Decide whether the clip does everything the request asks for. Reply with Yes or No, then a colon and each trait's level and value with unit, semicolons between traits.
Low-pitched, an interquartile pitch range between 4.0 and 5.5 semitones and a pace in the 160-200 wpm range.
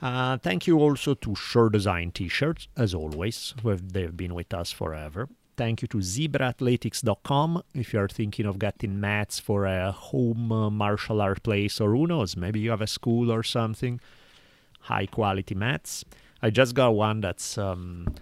No: low, 110 Hz; average, 3.6 semitones; average, 180 wpm